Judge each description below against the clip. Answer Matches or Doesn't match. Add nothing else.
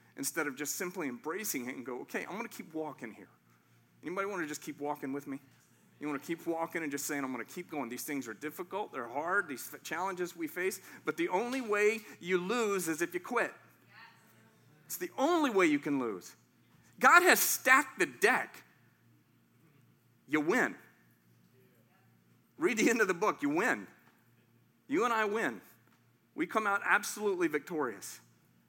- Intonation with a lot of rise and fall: Matches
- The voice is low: Doesn't match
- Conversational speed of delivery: Matches